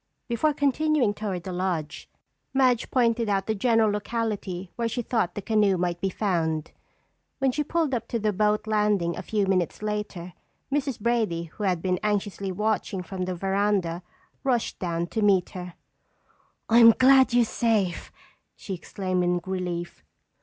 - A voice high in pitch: Yes, high, 205 Hz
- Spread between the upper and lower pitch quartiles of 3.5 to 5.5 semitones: Yes, average, 4.0 semitones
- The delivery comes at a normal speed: Yes, average, 160 wpm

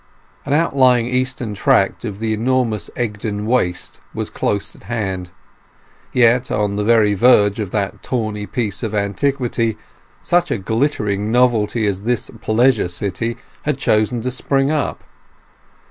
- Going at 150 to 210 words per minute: No, average, 140 wpm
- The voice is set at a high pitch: No, low, 115 Hz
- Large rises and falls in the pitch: No, average, 3.4 semitones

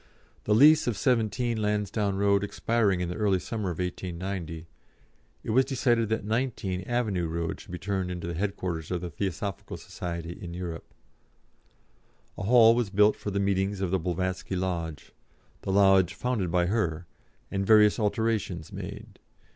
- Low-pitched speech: Yes, very low, 95 Hz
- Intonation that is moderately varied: Yes, average, 3.3 semitones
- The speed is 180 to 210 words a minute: No, average, 160 wpm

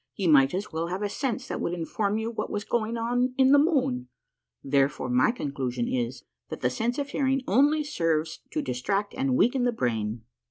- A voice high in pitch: Yes, high, 205 Hz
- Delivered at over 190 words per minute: Yes, average, 200 wpm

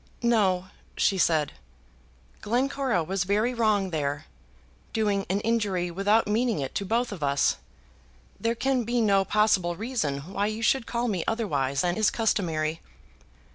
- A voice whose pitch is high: Yes, high, 200 Hz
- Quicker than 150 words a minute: No, average, 145 wpm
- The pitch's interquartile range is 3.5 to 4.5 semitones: No, wide, 5.4 semitones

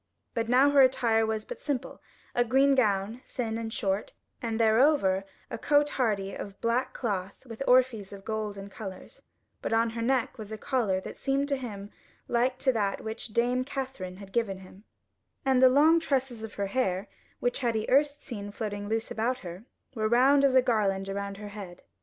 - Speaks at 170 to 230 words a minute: Yes, average, 195 wpm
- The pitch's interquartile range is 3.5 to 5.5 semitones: Yes, average, 4.2 semitones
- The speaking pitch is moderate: No, high, 225 Hz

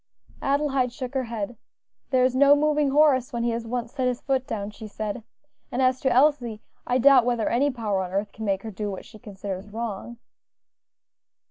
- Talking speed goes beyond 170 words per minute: Yes, average, 200 wpm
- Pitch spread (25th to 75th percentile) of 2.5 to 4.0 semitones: Yes, average, 3.6 semitones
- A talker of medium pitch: No, high, 240 Hz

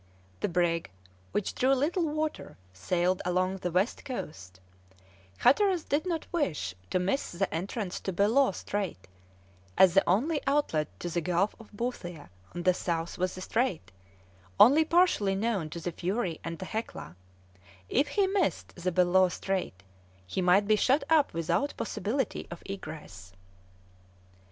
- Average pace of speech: Yes, average, 150 wpm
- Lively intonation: Yes, wide, 7.1 semitones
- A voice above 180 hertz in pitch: Yes, high, 190 Hz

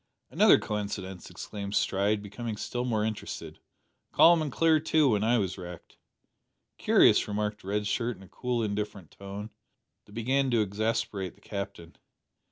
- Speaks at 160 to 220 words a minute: No, average, 150 wpm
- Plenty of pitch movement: No, average, 3.1 semitones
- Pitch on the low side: Yes, low, 105 Hz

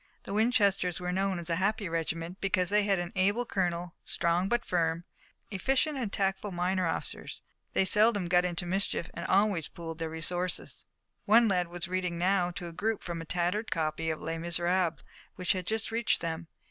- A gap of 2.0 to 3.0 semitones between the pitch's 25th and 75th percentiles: Yes, average, 2.7 semitones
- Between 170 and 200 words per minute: Yes, average, 190 wpm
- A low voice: No, medium, 180 Hz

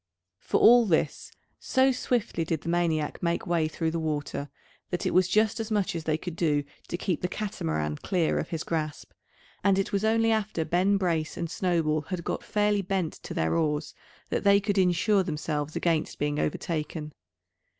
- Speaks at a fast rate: No, average, 185 wpm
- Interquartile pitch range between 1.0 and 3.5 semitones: No, average, 4.2 semitones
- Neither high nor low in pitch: Yes, medium, 170 Hz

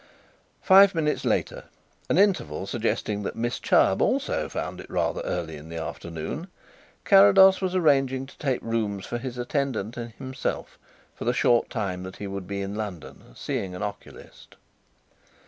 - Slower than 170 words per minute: Yes, average, 160 wpm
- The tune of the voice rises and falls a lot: Yes, wide, 6.1 semitones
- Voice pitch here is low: Yes, low, 115 Hz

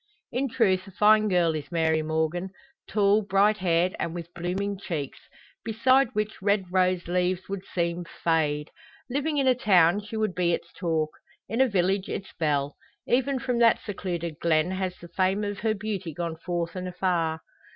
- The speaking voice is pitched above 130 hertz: Yes, medium, 185 Hz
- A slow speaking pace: No, average, 175 wpm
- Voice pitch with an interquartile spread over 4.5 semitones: No, average, 3.7 semitones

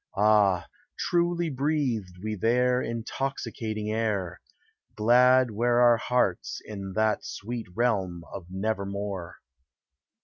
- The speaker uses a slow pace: Yes, slow, 105 wpm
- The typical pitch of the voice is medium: No, low, 110 Hz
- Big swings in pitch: No, average, 3.8 semitones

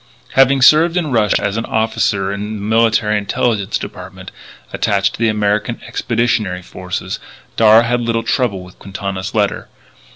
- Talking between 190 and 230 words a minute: No, average, 150 wpm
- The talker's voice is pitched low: Yes, low, 110 Hz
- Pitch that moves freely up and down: No, average, 2.7 semitones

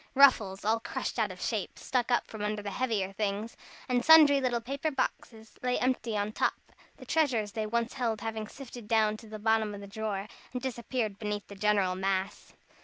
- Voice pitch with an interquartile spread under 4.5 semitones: Yes, average, 3.1 semitones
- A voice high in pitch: Yes, high, 220 Hz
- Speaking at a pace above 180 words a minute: Yes, average, 195 wpm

